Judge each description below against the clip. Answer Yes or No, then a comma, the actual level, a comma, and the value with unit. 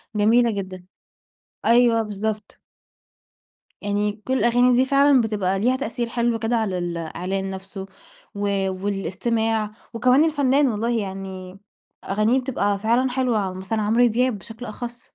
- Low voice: No, high, 220 Hz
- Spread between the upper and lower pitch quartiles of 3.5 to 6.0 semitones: Yes, average, 3.8 semitones